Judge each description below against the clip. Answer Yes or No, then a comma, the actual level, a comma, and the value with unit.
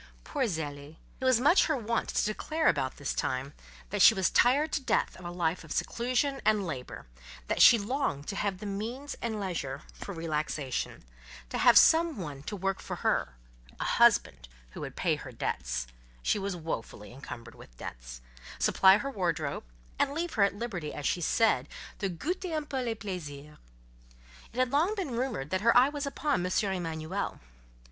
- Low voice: No, high, 195 Hz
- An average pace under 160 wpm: No, average, 185 wpm